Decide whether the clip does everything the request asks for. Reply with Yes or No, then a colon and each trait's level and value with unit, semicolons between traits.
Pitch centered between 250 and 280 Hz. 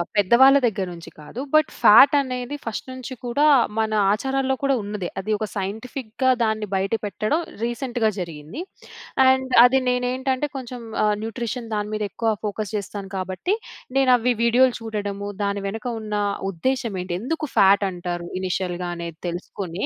No: high, 220 Hz